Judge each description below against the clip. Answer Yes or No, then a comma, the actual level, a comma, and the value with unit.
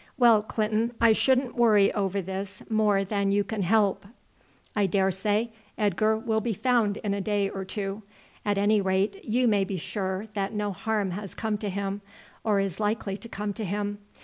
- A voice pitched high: Yes, high, 205 Hz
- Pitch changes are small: Yes, narrow, 1.8 semitones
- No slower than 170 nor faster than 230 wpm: Yes, average, 185 wpm